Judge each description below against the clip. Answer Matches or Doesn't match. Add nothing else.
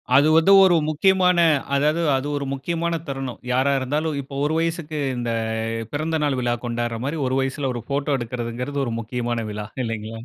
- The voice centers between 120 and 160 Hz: Matches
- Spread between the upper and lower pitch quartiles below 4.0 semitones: Doesn't match